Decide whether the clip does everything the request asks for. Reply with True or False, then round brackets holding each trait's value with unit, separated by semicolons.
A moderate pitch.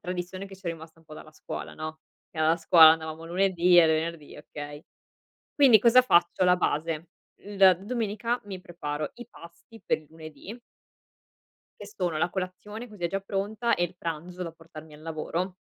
True (175 Hz)